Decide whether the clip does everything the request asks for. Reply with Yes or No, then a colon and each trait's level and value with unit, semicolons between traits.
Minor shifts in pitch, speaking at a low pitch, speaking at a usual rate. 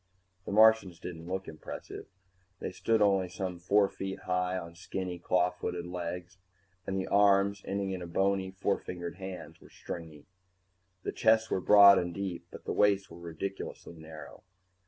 Yes: narrow, 2.1 semitones; very low, 95 Hz; average, 160 wpm